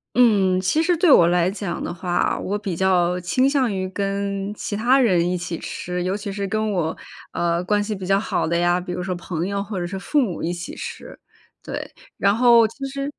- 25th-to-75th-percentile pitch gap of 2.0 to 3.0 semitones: No, average, 3.4 semitones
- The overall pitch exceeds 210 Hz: No, high, 195 Hz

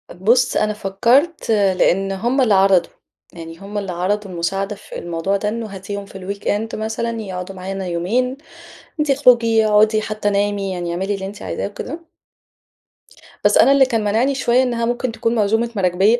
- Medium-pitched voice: No, high, 205 Hz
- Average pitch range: Yes, average, 3.4 semitones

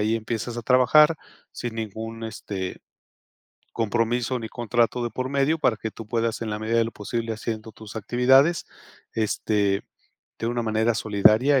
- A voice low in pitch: Yes, low, 115 Hz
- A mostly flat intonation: Yes, narrow, 1.9 semitones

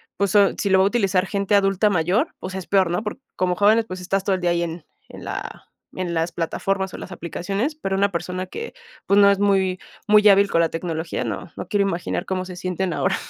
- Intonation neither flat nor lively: No, narrow, 2.2 semitones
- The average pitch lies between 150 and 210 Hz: Yes, high, 190 Hz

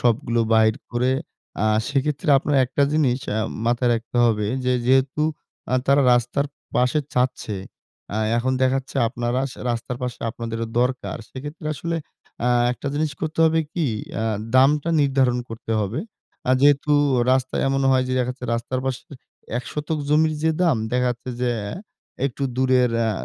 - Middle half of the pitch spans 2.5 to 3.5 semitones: Yes, average, 2.8 semitones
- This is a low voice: Yes, low, 130 Hz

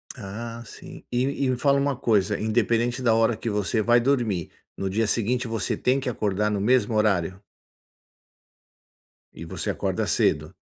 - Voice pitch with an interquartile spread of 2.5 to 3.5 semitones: Yes, average, 3.0 semitones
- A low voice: Yes, low, 115 Hz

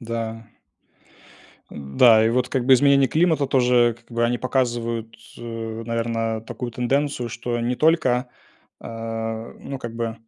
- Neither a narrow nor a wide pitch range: No, narrow, 1.9 semitones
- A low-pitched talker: Yes, low, 120 Hz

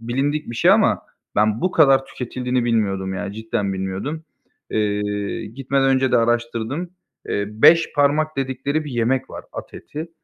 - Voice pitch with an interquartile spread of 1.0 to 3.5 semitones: No, average, 4.5 semitones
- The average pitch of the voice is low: Yes, low, 125 Hz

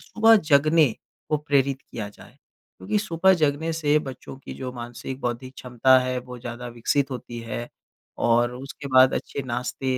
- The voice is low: Yes, low, 130 Hz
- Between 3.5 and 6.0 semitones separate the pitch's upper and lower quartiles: No, average, 3.1 semitones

